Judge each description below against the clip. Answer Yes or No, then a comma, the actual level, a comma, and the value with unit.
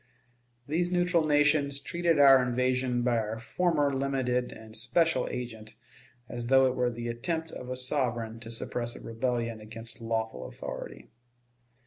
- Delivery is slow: No, average, 145 wpm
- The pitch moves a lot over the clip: No, average, 3.5 semitones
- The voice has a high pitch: No, low, 125 Hz